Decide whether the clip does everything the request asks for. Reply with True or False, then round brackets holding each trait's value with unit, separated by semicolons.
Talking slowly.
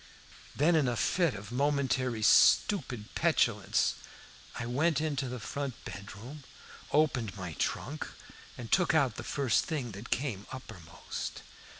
True (130 wpm)